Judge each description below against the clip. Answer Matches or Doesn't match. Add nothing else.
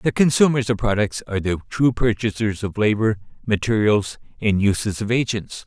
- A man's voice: Matches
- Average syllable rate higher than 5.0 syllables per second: Matches